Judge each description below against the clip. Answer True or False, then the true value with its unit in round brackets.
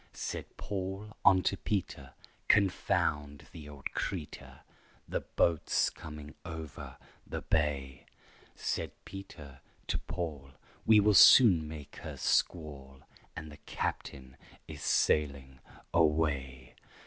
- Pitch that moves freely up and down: False (4.5 semitones)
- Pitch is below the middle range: True (75 Hz)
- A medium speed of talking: False (105 wpm)